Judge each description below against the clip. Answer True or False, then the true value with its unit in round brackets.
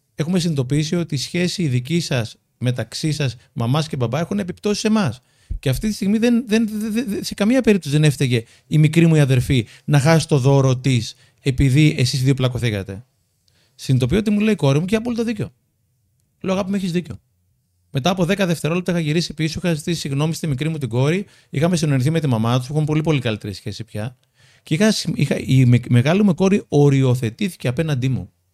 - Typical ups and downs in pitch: False (6.0 semitones)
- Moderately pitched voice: True (145 Hz)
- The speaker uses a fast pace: True (205 wpm)